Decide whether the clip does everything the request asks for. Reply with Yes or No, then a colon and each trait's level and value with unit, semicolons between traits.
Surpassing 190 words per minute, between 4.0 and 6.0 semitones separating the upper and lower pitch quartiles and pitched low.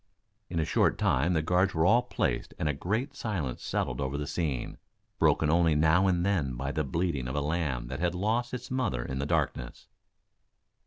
Yes: average, 200 wpm; average, 4.8 semitones; very low, 80 Hz